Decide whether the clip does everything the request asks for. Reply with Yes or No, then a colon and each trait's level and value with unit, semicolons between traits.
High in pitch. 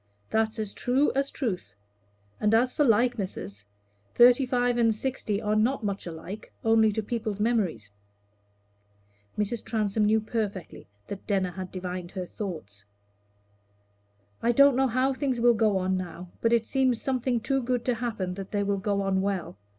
Yes: high, 220 Hz